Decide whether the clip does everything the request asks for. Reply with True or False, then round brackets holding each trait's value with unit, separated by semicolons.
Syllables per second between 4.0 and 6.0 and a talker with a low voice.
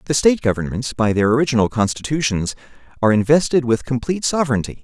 False (6.9 syllables/s; 130 Hz)